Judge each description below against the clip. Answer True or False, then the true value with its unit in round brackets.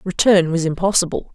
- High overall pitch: False (180 Hz)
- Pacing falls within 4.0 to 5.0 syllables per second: False (5.7 syllables/s)